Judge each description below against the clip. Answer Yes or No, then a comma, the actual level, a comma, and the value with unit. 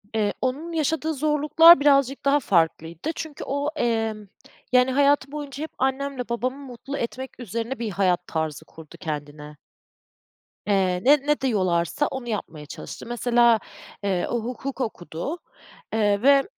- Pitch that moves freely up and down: Yes, wide, 6.1 semitones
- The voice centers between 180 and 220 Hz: No, high, 245 Hz